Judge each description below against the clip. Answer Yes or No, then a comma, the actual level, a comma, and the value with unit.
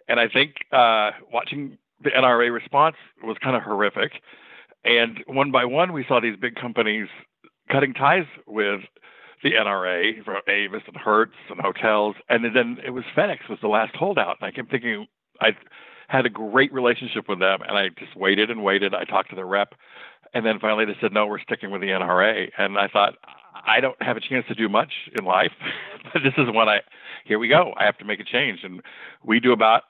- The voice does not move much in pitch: No, average, 3.0 semitones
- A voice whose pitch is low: Yes, low, 120 Hz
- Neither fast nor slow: No, fast, 210 wpm